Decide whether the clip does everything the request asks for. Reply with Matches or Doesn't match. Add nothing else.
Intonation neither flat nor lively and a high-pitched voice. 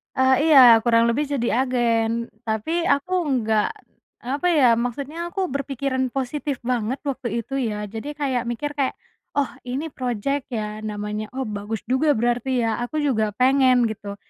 Matches